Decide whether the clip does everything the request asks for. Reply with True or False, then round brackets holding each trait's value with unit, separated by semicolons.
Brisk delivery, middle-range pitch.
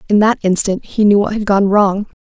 False (240 wpm; 205 Hz)